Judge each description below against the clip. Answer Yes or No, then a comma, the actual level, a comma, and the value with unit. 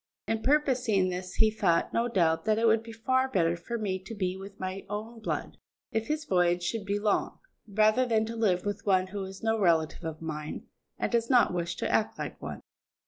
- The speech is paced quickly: Yes, fast, 215 wpm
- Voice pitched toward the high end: Yes, high, 205 Hz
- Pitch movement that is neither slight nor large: Yes, average, 3.6 semitones